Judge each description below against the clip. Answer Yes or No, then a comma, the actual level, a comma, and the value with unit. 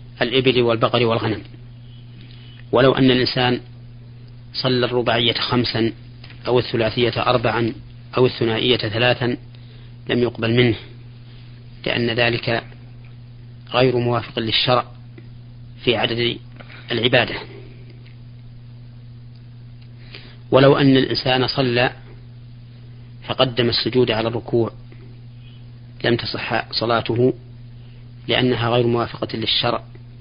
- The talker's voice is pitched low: Yes, low, 120 Hz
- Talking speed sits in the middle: Yes, average, 80 wpm